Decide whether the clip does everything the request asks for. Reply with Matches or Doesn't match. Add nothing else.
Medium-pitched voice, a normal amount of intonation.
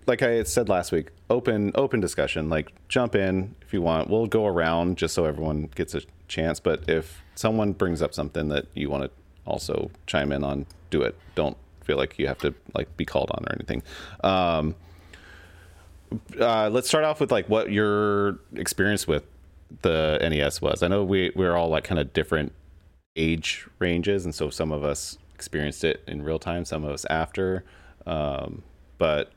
Doesn't match